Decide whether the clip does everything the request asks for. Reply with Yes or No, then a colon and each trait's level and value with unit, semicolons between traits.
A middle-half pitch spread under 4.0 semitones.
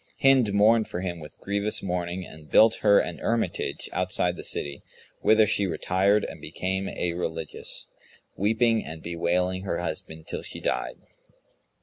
Yes: average, 3.5 semitones